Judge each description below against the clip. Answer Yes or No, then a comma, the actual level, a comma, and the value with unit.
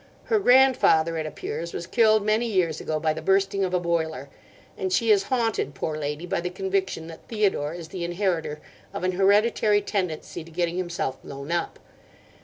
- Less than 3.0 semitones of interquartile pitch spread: No, average, 4.0 semitones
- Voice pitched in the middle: Yes, medium, 180 Hz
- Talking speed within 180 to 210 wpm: Yes, average, 185 wpm